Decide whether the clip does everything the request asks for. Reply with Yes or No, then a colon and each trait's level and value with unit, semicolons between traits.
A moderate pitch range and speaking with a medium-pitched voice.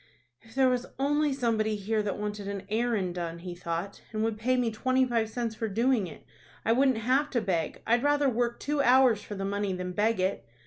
No: average, 4.0 semitones; high, 225 Hz